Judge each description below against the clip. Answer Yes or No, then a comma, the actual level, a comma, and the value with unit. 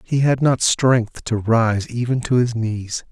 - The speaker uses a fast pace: No, average, 195 wpm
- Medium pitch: No, low, 120 Hz